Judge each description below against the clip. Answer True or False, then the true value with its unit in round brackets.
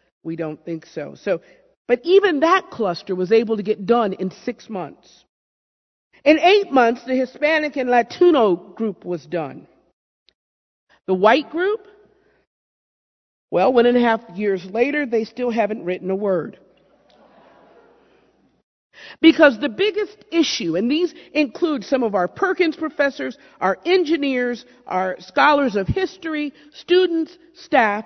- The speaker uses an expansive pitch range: True (8.5 semitones)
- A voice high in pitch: True (255 Hz)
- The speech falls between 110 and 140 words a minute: True (135 wpm)